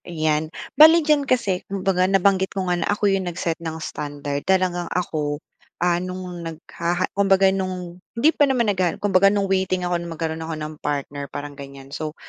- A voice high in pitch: No, medium, 180 Hz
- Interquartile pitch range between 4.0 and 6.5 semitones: No, average, 3.3 semitones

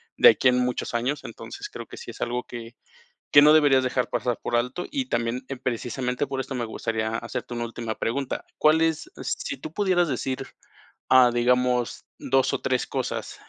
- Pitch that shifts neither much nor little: Yes, average, 3.2 semitones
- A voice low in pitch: Yes, low, 125 Hz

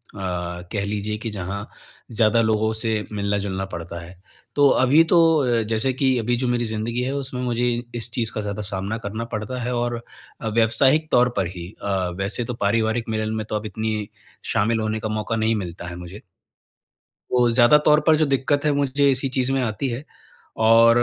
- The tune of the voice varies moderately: Yes, average, 3.3 semitones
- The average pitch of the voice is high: No, low, 110 Hz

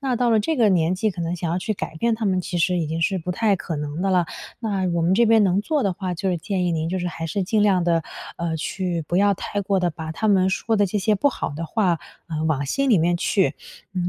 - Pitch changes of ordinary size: Yes, average, 3.5 semitones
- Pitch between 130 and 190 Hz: Yes, medium, 185 Hz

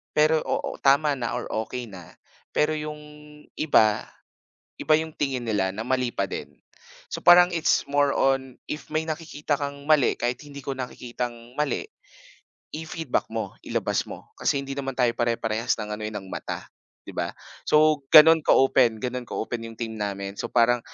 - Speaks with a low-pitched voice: Yes, low, 130 Hz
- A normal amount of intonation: Yes, average, 4.7 semitones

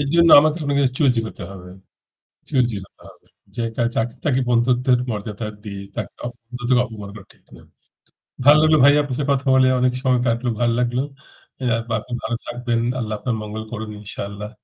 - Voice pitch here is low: Yes, low, 120 Hz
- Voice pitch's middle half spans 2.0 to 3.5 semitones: Yes, average, 3.1 semitones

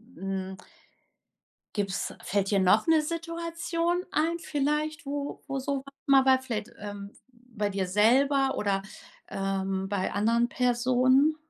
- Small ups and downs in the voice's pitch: No, wide, 6.3 semitones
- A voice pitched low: No, very high, 250 Hz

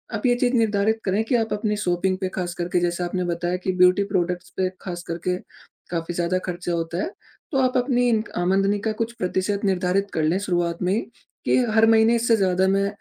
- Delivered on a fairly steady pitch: No, average, 3.7 semitones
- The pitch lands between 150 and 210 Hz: Yes, high, 190 Hz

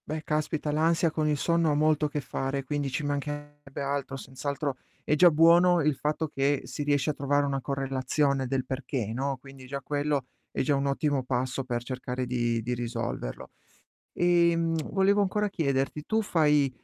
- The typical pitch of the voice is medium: Yes, medium, 145 Hz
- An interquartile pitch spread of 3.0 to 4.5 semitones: No, narrow, 2.4 semitones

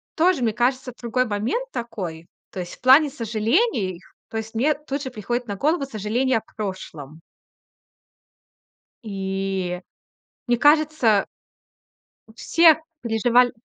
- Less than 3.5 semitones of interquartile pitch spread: No, average, 5.1 semitones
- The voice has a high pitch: Yes, high, 235 Hz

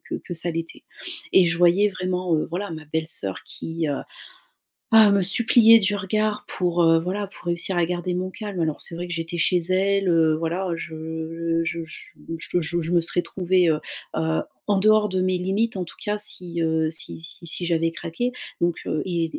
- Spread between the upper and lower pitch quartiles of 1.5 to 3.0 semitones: Yes, narrow, 2.5 semitones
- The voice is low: No, medium, 175 Hz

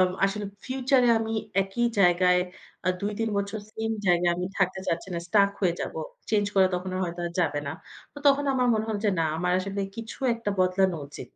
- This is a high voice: Yes, high, 195 Hz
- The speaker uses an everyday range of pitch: Yes, average, 3.7 semitones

